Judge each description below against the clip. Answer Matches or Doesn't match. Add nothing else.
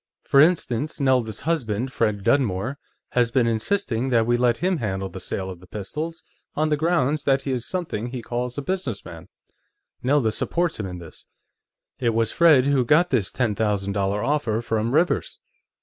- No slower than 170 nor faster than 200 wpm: Matches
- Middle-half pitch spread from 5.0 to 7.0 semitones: Matches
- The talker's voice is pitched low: Matches